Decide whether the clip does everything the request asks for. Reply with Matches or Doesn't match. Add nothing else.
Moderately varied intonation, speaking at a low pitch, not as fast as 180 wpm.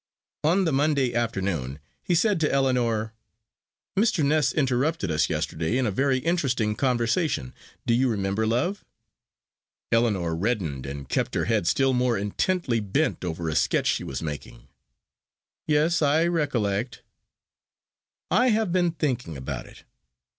Doesn't match